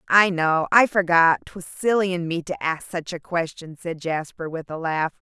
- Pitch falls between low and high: Yes, medium, 170 Hz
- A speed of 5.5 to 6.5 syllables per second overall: No, 4.9 syllables/s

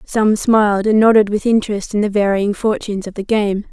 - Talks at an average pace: No, fast, 210 wpm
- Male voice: No, female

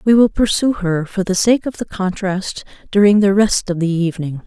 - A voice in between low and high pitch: No, high, 195 Hz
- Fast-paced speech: Yes, fast, 215 wpm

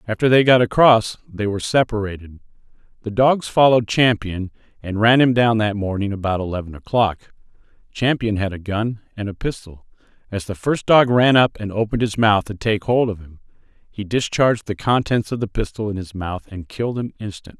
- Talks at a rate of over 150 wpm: Yes, average, 190 wpm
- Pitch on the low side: Yes, low, 110 Hz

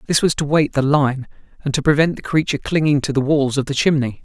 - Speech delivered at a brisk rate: Yes, fast, 255 wpm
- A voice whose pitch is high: No, medium, 145 Hz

